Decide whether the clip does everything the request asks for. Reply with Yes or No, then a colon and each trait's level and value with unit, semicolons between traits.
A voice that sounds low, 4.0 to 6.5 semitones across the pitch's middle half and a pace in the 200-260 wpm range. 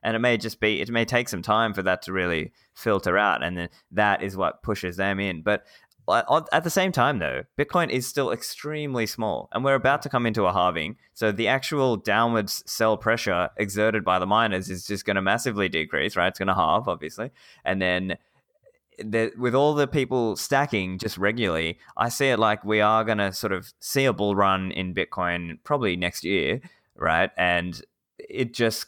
Yes: low, 110 Hz; average, 4.7 semitones; fast, 205 wpm